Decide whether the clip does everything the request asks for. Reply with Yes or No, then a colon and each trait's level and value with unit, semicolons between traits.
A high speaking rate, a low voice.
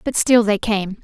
No: fast, 230 wpm; high, 215 Hz